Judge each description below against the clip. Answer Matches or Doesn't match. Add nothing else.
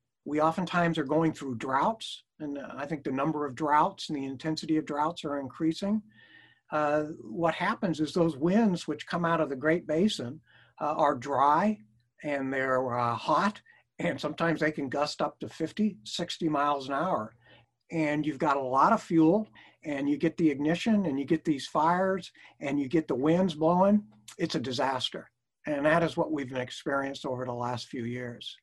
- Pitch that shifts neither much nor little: Matches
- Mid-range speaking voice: Matches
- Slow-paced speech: Doesn't match